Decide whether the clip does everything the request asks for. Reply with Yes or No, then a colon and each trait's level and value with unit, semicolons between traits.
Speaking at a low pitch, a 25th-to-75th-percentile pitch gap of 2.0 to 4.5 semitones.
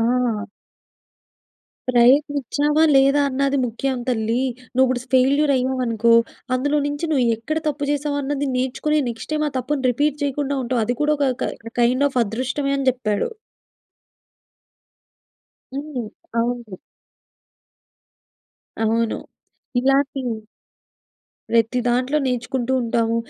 No: very high, 260 Hz; average, 3.1 semitones